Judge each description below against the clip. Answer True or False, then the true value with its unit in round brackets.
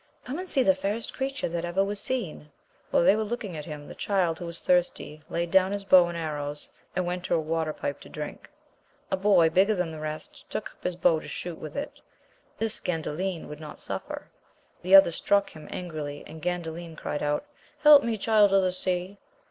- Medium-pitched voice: True (180 Hz)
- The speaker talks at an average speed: False (215 wpm)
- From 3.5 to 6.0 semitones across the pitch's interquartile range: True (3.9 semitones)